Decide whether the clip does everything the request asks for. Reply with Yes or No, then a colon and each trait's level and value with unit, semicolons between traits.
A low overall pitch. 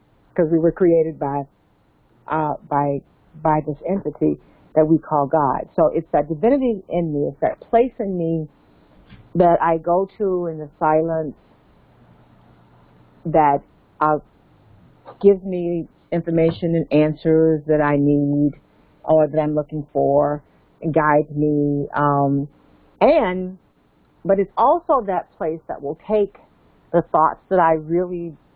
No: medium, 155 Hz